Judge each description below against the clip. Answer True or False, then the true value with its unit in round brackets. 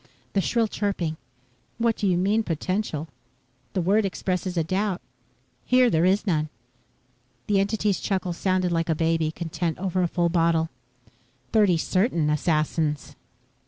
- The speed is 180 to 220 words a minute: False (140 wpm)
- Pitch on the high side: False (180 Hz)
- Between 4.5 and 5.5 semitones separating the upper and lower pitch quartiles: False (3.4 semitones)